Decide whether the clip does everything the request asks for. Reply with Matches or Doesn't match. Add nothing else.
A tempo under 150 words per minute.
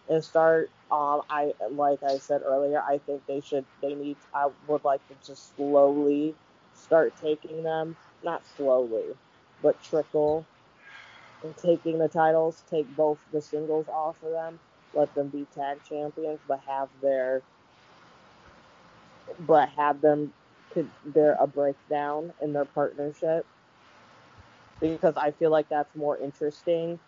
Matches